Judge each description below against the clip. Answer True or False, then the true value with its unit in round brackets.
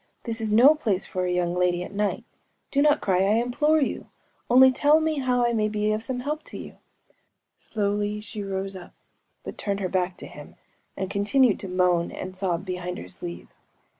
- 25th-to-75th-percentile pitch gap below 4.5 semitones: False (5.1 semitones)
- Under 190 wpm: False (195 wpm)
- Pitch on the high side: True (205 Hz)